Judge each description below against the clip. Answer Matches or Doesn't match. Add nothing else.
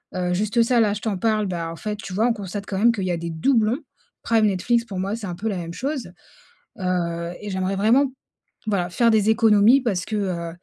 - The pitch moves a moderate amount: Matches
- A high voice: Matches